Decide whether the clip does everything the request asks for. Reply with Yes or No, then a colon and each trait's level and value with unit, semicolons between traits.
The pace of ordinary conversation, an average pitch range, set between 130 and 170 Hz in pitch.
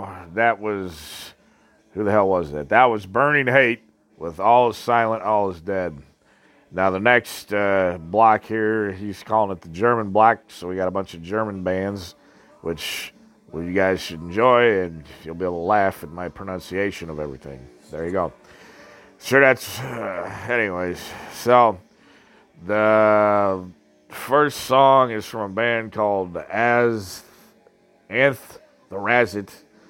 No: average, 155 wpm; average, 4.2 semitones; low, 100 Hz